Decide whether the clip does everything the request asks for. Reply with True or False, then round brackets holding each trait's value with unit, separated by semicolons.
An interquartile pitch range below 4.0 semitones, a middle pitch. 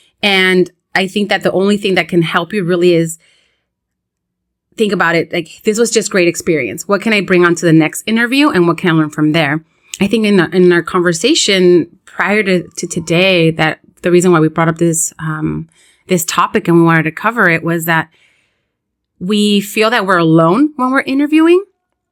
True (3.6 semitones; 180 Hz)